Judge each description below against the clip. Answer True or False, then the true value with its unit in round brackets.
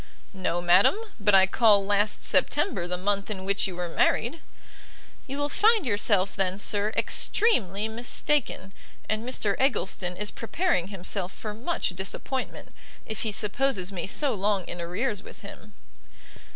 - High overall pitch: True (205 Hz)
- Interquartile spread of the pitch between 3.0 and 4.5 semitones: True (3.6 semitones)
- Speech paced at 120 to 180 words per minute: True (150 wpm)